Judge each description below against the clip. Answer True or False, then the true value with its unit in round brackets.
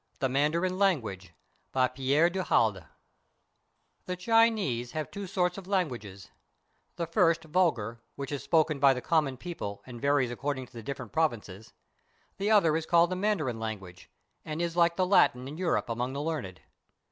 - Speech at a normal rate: True (170 wpm)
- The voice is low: False (145 Hz)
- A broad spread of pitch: True (6.4 semitones)